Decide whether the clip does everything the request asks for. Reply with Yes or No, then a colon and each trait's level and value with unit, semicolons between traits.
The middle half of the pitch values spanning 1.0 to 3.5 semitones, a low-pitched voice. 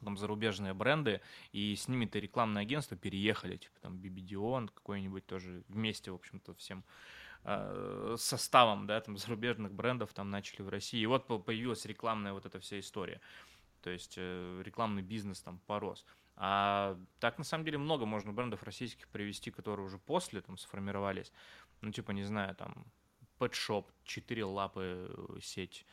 Yes: narrow, 2.6 semitones; low, 105 Hz